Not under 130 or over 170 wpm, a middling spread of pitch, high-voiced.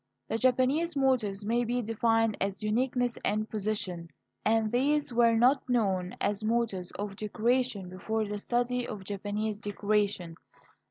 Yes: average, 140 wpm; average, 3.1 semitones; high, 220 Hz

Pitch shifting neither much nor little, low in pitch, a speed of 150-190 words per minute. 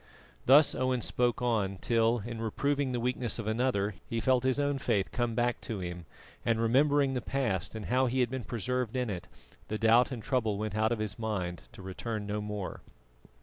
No: average, 3.2 semitones; low, 115 Hz; average, 200 wpm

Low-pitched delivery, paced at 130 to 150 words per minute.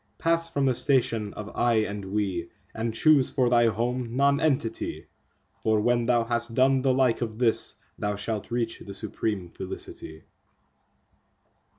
Yes: low, 115 Hz; average, 145 wpm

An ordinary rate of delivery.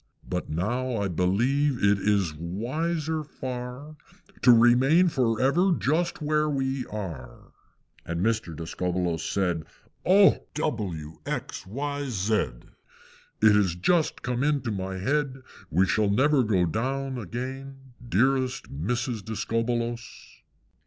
No: slow, 120 wpm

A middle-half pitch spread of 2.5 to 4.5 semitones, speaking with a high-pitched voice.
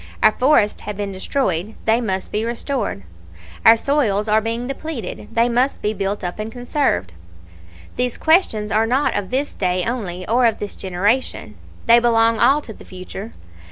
Yes: average, 3.7 semitones; high, 225 Hz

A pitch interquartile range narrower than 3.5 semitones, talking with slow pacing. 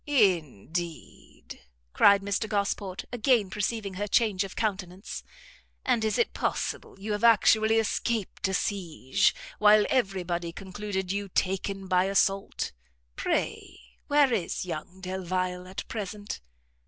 Yes: narrow, 2.6 semitones; slow, 125 wpm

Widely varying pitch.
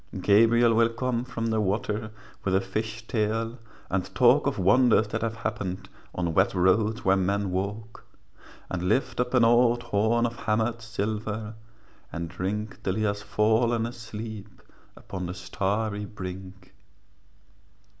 No: average, 3.0 semitones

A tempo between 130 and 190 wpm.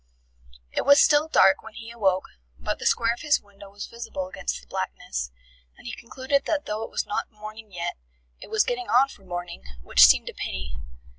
No: fast, 205 wpm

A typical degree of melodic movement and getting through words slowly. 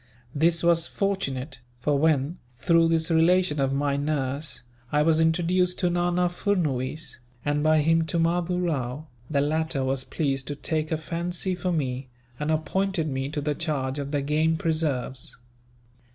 No: average, 3.2 semitones; average, 160 wpm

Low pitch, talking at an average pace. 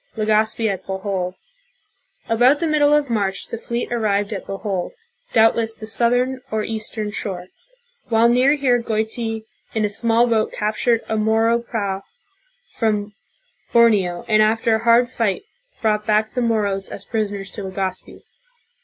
No: high, 220 Hz; average, 170 wpm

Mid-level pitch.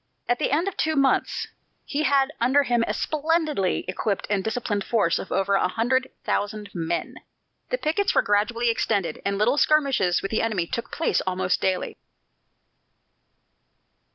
No: high, 230 Hz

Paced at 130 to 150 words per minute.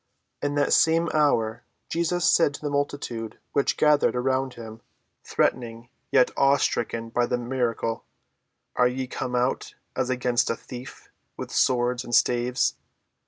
Yes: average, 140 wpm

